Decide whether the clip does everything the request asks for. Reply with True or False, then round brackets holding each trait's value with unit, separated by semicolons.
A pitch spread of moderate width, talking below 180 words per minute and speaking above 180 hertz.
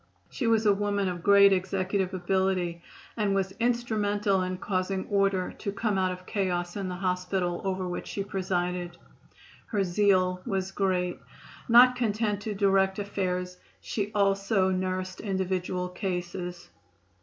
False (1.8 semitones; 140 wpm; 190 Hz)